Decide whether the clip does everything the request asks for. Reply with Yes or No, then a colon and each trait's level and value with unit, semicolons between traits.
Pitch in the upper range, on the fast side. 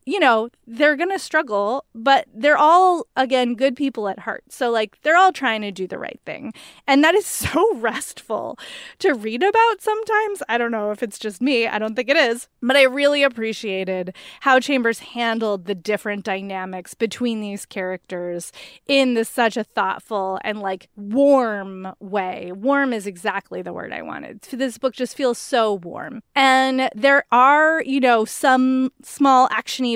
No: high, 245 Hz; average, 175 wpm